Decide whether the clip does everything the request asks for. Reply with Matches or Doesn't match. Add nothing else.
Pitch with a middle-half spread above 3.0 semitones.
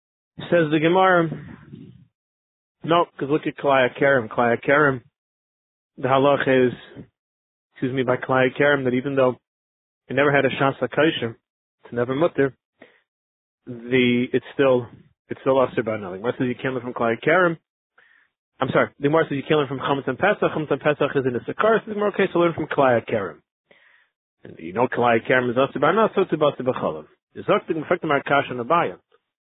Matches